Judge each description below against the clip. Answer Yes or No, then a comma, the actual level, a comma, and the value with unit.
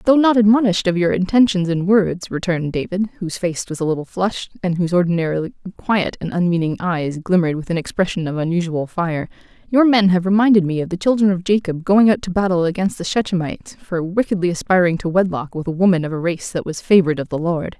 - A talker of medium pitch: Yes, medium, 180 Hz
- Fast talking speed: Yes, fast, 215 wpm